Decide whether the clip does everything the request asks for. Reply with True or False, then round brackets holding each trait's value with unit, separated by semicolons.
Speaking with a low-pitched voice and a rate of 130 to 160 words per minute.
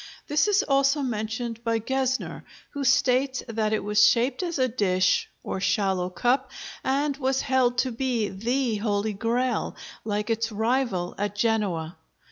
False (230 Hz; 150 wpm)